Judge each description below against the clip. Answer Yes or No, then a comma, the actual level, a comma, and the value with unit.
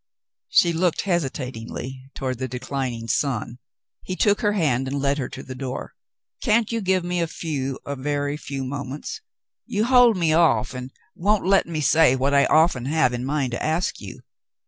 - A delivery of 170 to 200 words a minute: Yes, average, 190 wpm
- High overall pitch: No, medium, 145 Hz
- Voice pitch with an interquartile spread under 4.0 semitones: No, average, 4.9 semitones